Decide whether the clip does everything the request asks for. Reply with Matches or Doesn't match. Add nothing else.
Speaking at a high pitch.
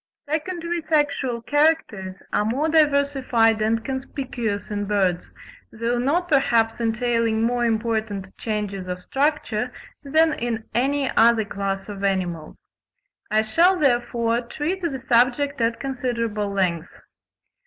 Matches